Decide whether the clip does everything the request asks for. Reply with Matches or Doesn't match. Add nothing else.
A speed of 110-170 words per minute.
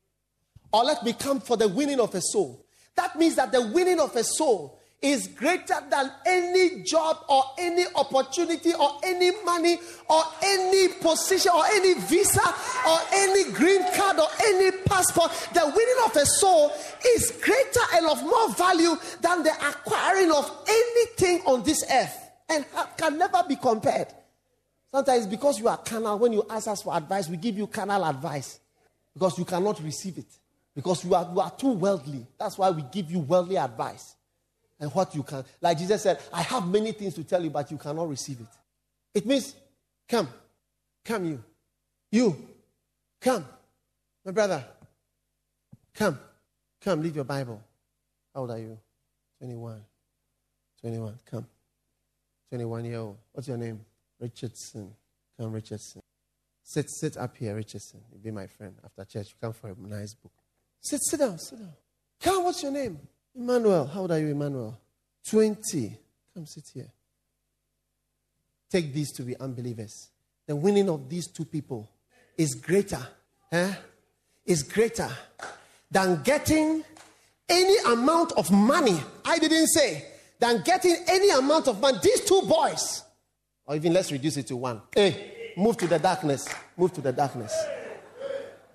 Matches